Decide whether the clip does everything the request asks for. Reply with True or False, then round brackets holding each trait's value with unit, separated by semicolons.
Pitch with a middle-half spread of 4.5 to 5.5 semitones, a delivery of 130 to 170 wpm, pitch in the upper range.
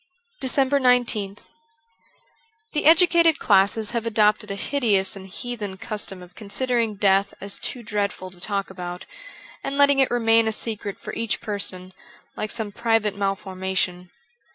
False (3.6 semitones; 150 wpm; 210 Hz)